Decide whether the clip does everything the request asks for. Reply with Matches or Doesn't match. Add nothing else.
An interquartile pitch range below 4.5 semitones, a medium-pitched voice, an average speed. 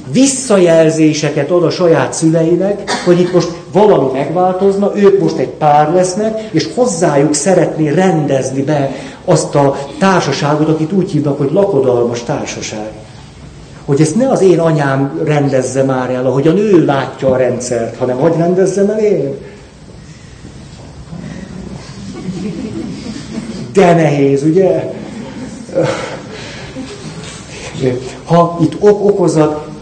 Doesn't match